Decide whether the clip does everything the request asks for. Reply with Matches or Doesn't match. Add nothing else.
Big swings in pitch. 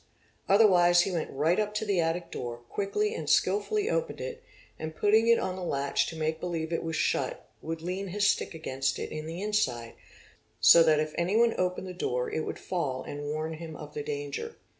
Doesn't match